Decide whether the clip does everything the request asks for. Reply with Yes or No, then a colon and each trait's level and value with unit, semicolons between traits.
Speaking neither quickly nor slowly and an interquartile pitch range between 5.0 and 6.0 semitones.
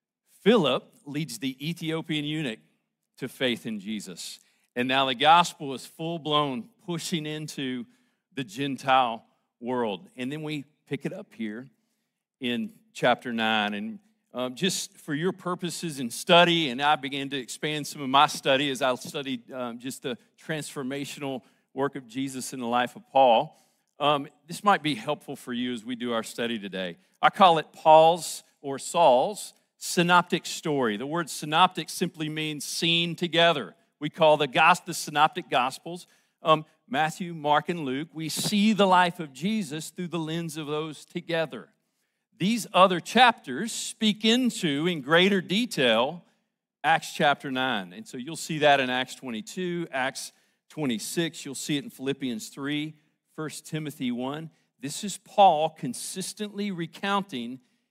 Yes: average, 155 wpm; average, 5.3 semitones